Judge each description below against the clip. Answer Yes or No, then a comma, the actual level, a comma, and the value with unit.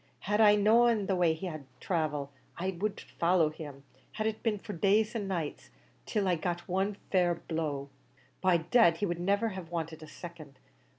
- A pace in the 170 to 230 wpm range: Yes, average, 190 wpm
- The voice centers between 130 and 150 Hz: No, medium, 175 Hz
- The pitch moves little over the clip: No, average, 4.1 semitones